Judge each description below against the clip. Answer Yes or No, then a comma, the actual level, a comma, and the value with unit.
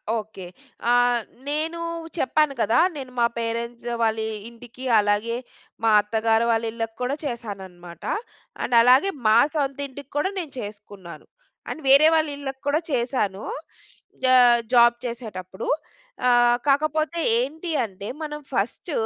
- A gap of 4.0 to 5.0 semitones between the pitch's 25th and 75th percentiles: Yes, average, 4.3 semitones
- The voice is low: No, high, 240 Hz